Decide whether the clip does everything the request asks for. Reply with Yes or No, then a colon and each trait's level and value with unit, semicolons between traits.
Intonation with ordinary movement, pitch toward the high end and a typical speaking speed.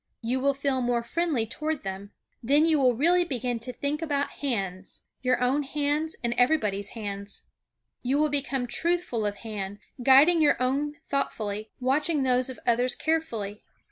Yes: average, 4.4 semitones; very high, 260 Hz; average, 160 wpm